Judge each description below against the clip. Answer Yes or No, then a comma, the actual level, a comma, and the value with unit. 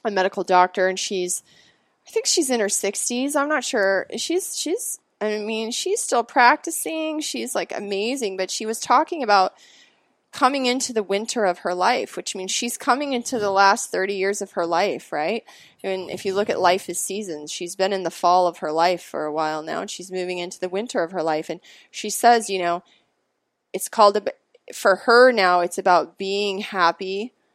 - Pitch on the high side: Yes, high, 195 Hz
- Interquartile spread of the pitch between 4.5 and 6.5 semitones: Yes, average, 4.8 semitones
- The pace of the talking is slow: No, fast, 205 wpm